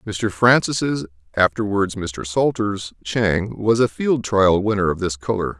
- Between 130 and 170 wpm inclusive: Yes, average, 150 wpm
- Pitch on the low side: Yes, low, 105 Hz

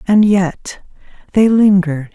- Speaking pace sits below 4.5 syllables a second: Yes, 4.1 syllables/s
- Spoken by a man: No, female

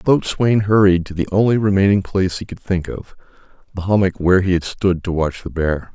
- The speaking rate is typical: No, fast, 220 wpm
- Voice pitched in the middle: No, very low, 95 Hz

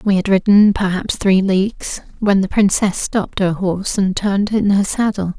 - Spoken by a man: No, female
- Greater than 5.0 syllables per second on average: No, 4.9 syllables/s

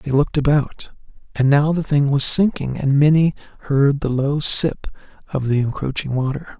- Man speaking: Yes, male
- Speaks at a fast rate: No, average, 175 wpm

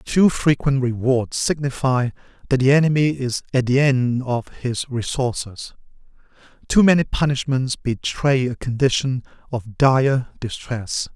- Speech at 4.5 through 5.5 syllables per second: No, 4.1 syllables/s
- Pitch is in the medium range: No, low, 130 Hz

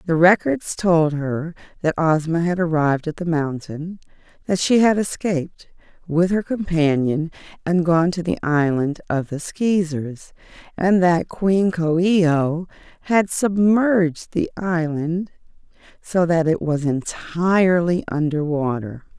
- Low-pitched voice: No, medium, 170 Hz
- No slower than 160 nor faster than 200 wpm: No, slow, 135 wpm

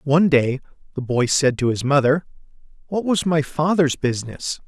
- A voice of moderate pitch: Yes, medium, 145 Hz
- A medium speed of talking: Yes, average, 165 wpm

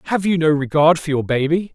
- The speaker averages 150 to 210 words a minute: No, fast, 240 wpm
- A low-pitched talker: No, medium, 160 Hz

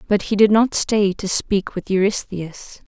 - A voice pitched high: Yes, high, 200 Hz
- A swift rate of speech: No, average, 185 wpm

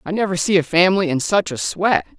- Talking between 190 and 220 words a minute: No, fast, 245 wpm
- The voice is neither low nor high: Yes, medium, 180 Hz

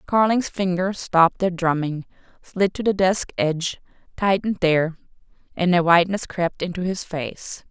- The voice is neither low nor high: Yes, medium, 180 Hz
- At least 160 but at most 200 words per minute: No, average, 150 wpm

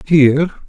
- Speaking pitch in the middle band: Yes, medium, 150 Hz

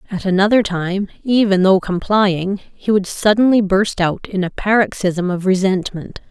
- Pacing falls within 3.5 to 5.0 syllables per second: Yes, 4.5 syllables/s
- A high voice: Yes, high, 195 Hz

